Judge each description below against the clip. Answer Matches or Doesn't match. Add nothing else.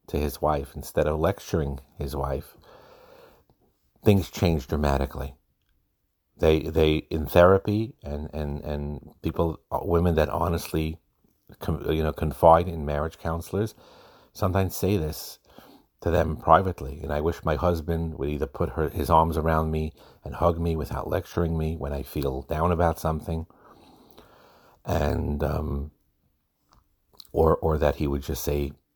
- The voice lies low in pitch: Matches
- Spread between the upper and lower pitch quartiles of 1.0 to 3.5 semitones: Matches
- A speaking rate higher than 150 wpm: Doesn't match